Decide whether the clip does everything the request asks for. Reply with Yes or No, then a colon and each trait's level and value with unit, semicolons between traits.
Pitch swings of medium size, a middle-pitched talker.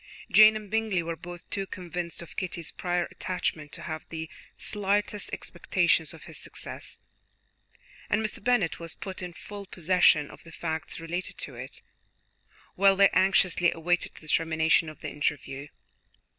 Yes: average, 3.3 semitones; medium, 175 Hz